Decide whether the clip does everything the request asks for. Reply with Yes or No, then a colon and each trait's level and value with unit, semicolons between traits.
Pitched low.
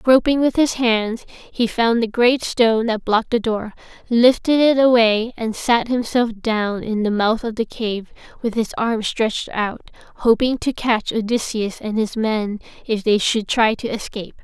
No: high, 225 Hz